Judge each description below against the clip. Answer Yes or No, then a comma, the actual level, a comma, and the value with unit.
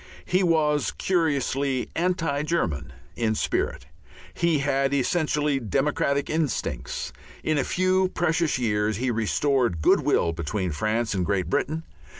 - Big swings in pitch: Yes, wide, 6.5 semitones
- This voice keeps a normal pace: No, slow, 130 wpm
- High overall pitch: No, medium, 140 Hz